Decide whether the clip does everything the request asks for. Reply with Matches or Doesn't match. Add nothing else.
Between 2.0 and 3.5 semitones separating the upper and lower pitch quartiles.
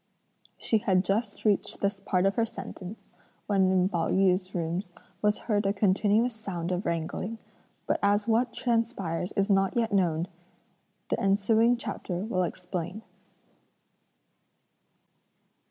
Matches